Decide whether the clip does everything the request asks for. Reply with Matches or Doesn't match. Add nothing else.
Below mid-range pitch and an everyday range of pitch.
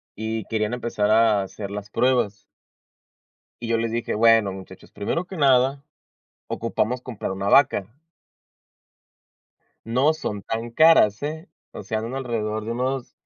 Matches